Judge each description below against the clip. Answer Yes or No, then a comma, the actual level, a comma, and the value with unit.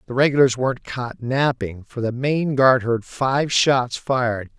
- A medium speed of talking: Yes, average, 170 wpm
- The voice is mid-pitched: No, low, 125 Hz